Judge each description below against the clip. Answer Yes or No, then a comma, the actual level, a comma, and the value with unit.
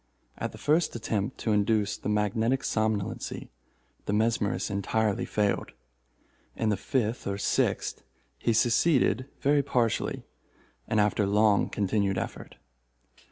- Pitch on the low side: Yes, low, 110 Hz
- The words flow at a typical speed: No, slow, 120 wpm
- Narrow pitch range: Yes, narrow, 2.3 semitones